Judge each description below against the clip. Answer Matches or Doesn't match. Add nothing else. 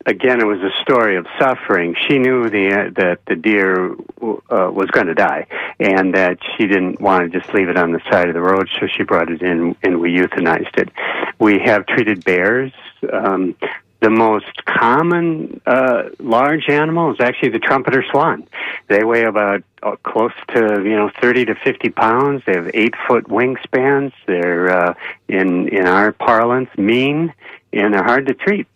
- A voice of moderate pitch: Doesn't match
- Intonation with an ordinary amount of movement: Doesn't match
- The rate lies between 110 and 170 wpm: Doesn't match